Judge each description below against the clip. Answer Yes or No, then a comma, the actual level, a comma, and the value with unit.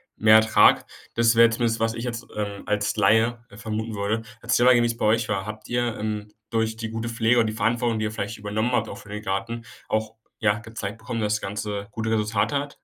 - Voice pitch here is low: Yes, low, 110 Hz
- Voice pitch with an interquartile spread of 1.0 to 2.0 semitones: Yes, narrow, 1.6 semitones